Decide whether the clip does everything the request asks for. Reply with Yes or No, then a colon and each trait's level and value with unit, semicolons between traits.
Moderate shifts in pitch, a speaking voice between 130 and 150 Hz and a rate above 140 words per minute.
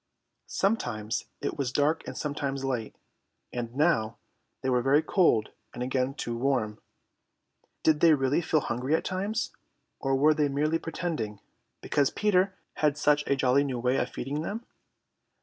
Yes: average, 3.8 semitones; medium, 140 Hz; average, 155 wpm